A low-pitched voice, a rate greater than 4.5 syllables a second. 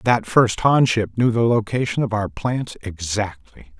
No: low, 110 Hz; 4.2 syllables/s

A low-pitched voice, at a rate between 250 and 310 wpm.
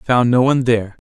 Yes: low, 120 Hz; fast, 280 wpm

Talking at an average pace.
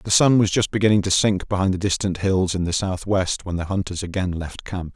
No: fast, 240 wpm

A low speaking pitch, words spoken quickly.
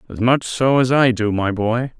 Yes: low, 120 Hz; fast, 240 wpm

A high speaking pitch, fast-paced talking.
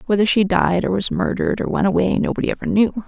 Yes: high, 205 Hz; fast, 235 wpm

